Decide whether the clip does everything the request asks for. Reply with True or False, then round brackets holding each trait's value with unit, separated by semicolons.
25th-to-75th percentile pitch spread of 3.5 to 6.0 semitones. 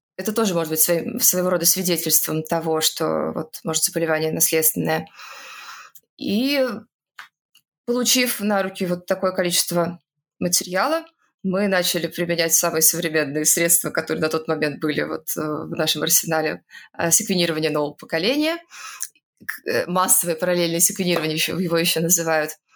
False (2.9 semitones)